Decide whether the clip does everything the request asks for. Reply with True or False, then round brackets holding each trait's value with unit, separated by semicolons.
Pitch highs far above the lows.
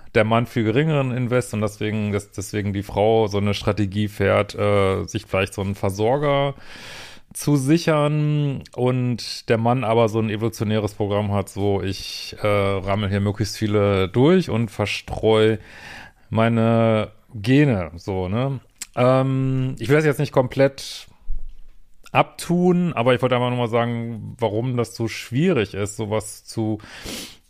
False (3.5 semitones)